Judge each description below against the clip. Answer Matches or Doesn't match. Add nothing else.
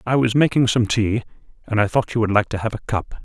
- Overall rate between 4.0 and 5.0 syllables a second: Doesn't match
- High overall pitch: Doesn't match